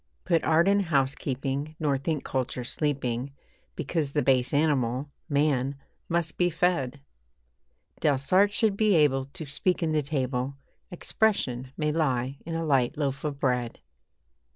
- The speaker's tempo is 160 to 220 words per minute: No, average, 140 wpm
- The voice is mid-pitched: Yes, medium, 145 Hz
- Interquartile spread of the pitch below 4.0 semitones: Yes, average, 3.6 semitones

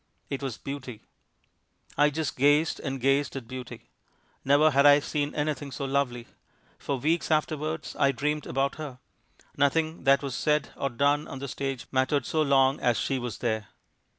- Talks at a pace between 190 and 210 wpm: No, average, 170 wpm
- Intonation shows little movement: Yes, narrow, 2.1 semitones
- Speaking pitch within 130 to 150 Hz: Yes, medium, 140 Hz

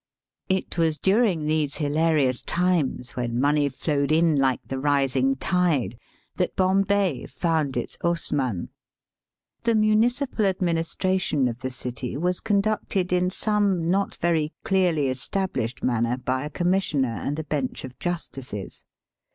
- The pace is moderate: No, slow, 130 wpm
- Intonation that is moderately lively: No, wide, 5.8 semitones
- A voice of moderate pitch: Yes, medium, 155 Hz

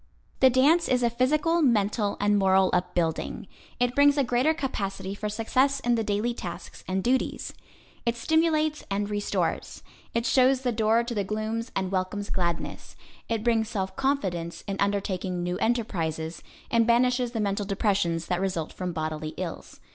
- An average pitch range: Yes, average, 4.6 semitones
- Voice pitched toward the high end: Yes, high, 215 Hz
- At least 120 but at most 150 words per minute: No, average, 160 wpm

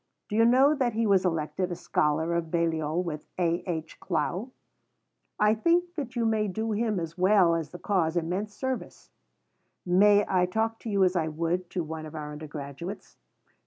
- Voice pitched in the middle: Yes, medium, 180 Hz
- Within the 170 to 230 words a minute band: Yes, average, 185 wpm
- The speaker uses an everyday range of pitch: Yes, average, 4.7 semitones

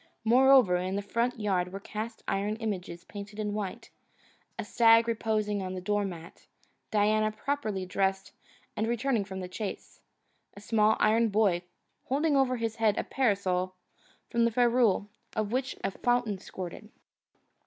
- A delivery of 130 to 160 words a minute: Yes, average, 150 wpm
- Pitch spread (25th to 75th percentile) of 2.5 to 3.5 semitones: Yes, average, 3.0 semitones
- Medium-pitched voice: No, high, 215 Hz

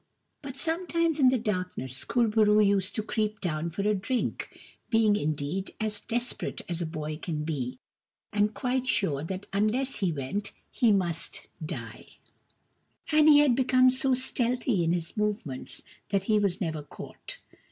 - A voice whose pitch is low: No, high, 210 Hz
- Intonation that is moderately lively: No, wide, 6.8 semitones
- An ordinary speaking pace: Yes, average, 165 wpm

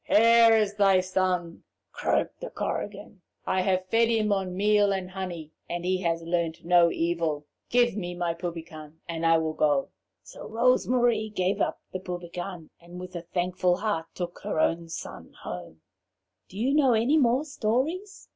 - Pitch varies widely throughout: No, average, 4.2 semitones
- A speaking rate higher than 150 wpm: Yes, average, 170 wpm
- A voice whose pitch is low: No, medium, 185 Hz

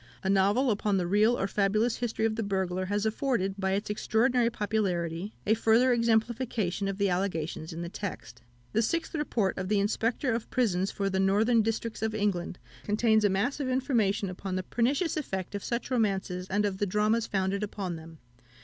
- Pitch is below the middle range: No, high, 205 Hz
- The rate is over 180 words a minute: Yes, average, 190 wpm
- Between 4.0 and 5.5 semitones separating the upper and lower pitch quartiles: No, average, 3.1 semitones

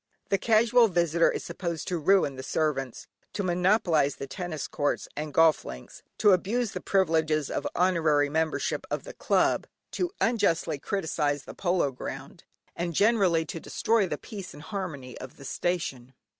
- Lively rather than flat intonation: No, average, 4.6 semitones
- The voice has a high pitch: No, medium, 170 Hz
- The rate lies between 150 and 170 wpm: Yes, average, 160 wpm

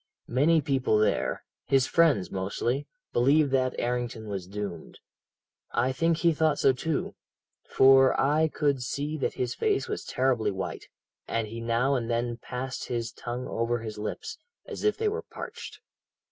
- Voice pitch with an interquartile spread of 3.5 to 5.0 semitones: Yes, average, 4.0 semitones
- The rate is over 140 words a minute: Yes, average, 160 wpm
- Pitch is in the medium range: No, low, 125 Hz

